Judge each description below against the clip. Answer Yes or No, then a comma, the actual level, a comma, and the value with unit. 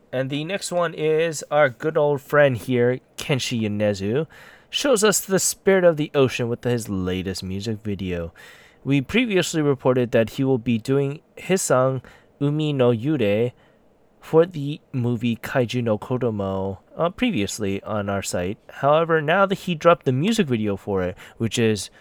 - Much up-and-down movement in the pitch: Yes, wide, 6.4 semitones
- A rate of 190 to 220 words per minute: No, average, 165 wpm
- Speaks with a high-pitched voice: No, low, 130 Hz